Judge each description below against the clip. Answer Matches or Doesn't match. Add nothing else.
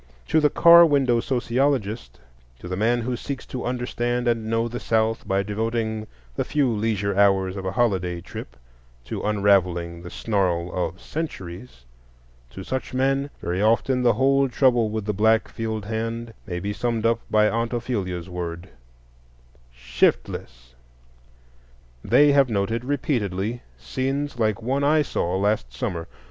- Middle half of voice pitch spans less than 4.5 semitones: Doesn't match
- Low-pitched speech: Matches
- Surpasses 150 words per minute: Doesn't match